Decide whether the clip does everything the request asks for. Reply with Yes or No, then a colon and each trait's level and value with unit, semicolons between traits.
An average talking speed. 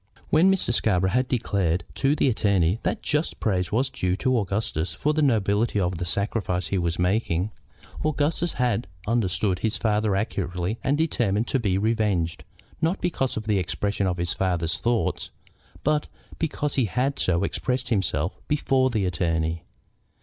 Yes: average, 160 wpm